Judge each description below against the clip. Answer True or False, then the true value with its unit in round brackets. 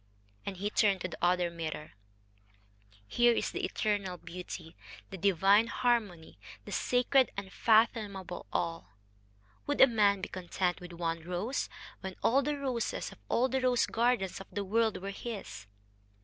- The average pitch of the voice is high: True (200 Hz)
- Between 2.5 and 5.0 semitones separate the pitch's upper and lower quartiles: True (4.6 semitones)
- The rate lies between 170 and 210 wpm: False (150 wpm)